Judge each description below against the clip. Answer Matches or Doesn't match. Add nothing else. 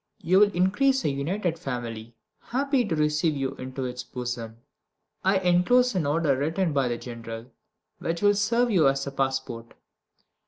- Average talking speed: Matches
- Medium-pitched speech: Matches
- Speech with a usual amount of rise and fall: Doesn't match